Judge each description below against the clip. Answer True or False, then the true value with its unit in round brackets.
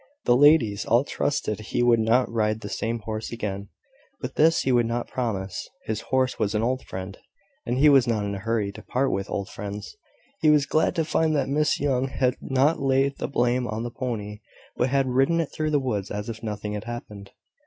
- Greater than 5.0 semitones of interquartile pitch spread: False (4.1 semitones)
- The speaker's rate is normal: False (215 wpm)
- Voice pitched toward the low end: True (120 Hz)